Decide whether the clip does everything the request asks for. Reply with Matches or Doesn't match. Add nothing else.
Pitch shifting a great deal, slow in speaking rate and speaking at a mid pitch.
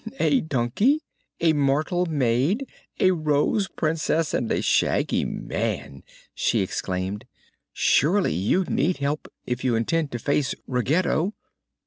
Matches